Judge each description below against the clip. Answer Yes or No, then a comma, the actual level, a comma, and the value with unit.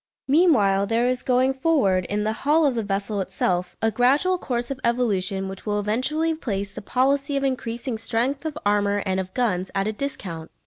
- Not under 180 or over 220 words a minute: Yes, average, 190 wpm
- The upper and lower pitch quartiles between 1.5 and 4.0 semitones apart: No, average, 5.2 semitones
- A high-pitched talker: Yes, high, 230 Hz